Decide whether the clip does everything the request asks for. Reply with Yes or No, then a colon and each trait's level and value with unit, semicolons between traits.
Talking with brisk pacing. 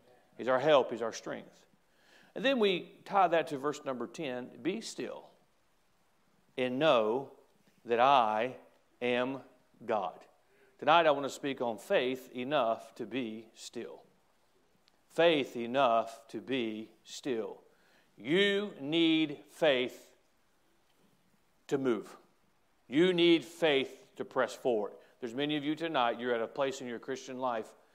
No: slow, 135 wpm